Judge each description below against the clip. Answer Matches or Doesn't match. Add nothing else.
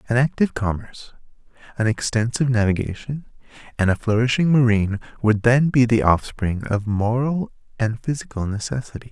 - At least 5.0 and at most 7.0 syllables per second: Matches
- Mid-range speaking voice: Doesn't match